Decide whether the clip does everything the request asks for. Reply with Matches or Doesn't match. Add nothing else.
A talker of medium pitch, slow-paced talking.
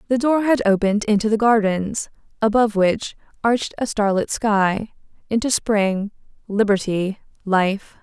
Doesn't match